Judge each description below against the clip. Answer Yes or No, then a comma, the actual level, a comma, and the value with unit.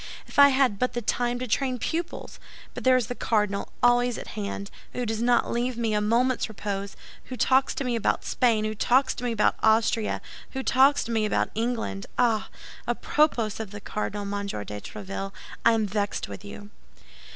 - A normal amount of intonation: Yes, average, 3.3 semitones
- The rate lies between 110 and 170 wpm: No, average, 195 wpm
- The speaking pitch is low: No, high, 225 Hz